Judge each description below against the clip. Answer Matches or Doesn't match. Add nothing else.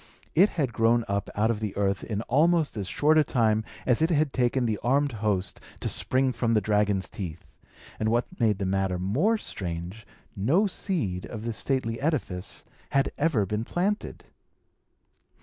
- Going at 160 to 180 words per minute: Matches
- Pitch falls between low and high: Doesn't match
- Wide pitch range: Matches